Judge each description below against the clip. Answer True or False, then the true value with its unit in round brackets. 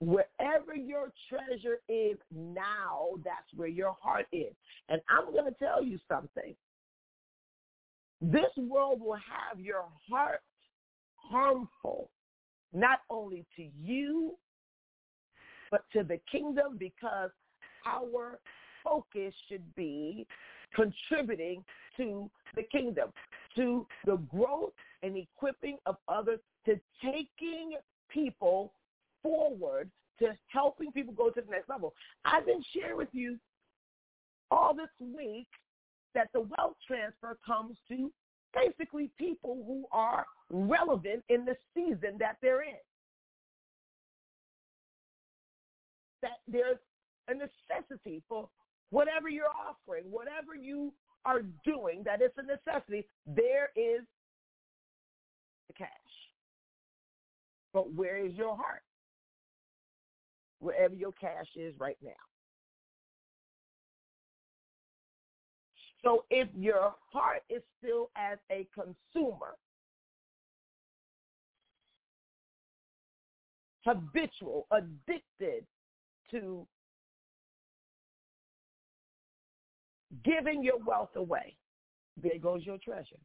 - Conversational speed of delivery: False (100 wpm)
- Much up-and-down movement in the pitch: True (6.6 semitones)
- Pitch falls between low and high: False (245 Hz)